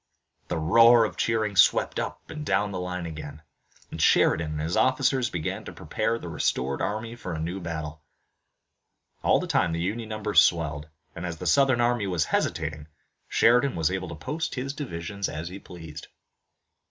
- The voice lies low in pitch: Yes, very low, 90 Hz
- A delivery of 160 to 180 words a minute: Yes, average, 175 wpm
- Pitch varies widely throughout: Yes, wide, 6.0 semitones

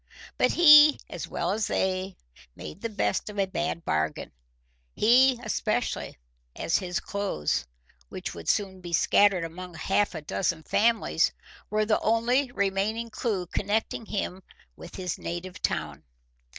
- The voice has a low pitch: No, high, 195 Hz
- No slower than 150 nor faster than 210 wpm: No, average, 140 wpm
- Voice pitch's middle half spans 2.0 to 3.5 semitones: No, average, 3.9 semitones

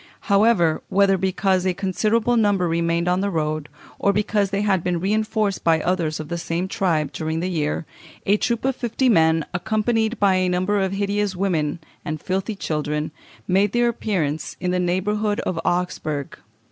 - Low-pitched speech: No, medium, 185 Hz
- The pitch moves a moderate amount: Yes, average, 3.7 semitones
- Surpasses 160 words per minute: Yes, average, 170 wpm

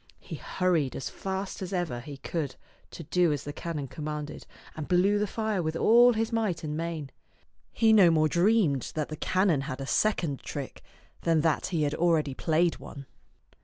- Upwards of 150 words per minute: Yes, average, 185 wpm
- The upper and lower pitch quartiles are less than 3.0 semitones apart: No, average, 4.2 semitones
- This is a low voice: No, medium, 165 Hz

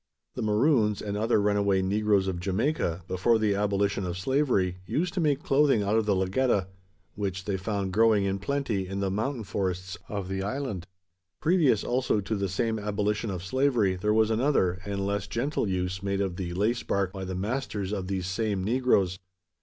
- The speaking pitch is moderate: No, low, 100 Hz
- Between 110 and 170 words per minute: No, average, 185 wpm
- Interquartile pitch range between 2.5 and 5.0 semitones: Yes, average, 3.0 semitones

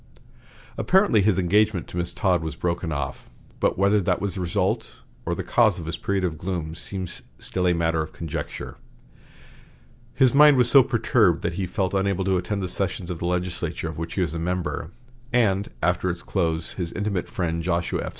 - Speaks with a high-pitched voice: No, very low, 90 Hz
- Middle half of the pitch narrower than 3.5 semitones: Yes, average, 2.8 semitones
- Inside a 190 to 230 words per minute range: Yes, average, 200 wpm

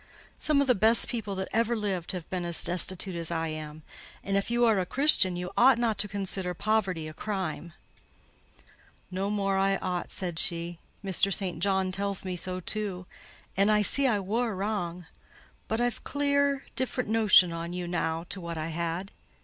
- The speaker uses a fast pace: No, average, 185 wpm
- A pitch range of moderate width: Yes, average, 3.6 semitones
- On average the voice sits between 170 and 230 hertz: Yes, high, 190 Hz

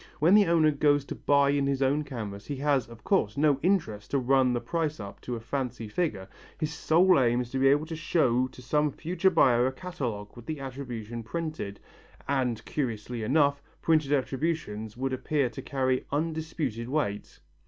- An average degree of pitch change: Yes, average, 4.2 semitones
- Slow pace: No, average, 185 wpm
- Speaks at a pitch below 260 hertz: Yes, low, 135 Hz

